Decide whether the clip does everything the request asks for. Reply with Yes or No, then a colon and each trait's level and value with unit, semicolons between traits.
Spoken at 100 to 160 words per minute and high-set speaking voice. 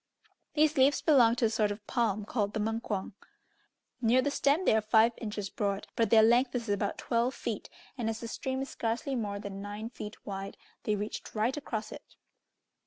No: average, 195 wpm; high, 225 Hz